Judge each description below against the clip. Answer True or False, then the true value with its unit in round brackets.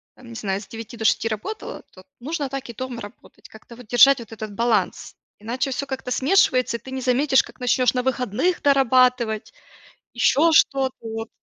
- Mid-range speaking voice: False (250 Hz)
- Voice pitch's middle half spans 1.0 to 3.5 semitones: True (2.9 semitones)